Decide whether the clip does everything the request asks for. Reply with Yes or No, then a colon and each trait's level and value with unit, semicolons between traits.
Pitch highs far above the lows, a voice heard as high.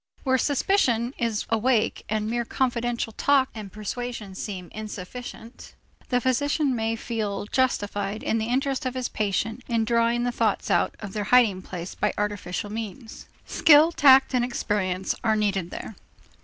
No: average, 3.2 semitones; high, 225 Hz